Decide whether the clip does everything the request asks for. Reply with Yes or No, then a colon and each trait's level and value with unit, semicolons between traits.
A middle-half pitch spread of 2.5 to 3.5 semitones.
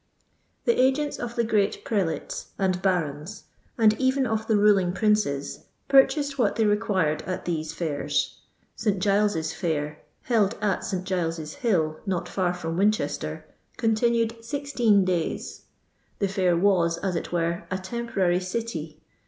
No: average, 4.8 semitones